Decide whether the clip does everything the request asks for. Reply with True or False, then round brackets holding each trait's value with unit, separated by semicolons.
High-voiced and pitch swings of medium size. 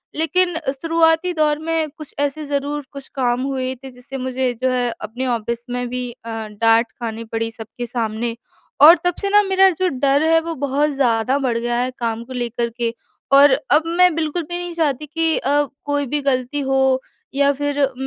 True (270 Hz; 4.1 semitones)